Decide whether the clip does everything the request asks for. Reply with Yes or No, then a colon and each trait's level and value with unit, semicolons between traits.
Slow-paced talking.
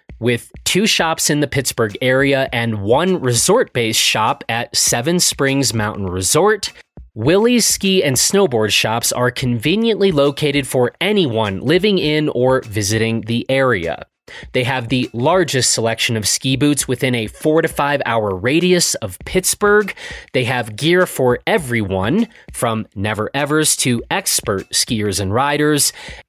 No: average, 145 wpm